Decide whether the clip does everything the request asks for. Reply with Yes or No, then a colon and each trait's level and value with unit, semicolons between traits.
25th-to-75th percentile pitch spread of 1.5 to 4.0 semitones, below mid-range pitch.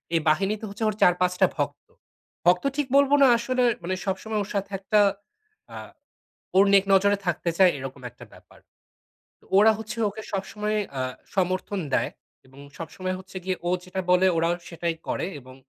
No: average, 2.9 semitones; high, 190 Hz